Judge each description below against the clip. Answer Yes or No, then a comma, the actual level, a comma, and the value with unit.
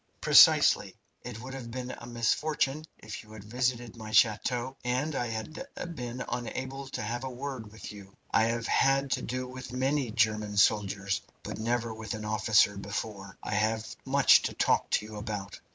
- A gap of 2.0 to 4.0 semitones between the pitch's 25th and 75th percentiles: Yes, average, 3.0 semitones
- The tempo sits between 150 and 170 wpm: No, average, 180 wpm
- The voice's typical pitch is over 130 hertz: No, low, 115 Hz